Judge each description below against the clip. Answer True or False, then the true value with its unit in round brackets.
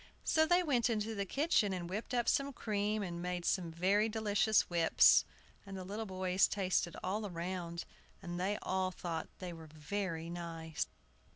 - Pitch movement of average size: True (3.6 semitones)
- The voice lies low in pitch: False (190 Hz)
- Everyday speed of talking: True (170 wpm)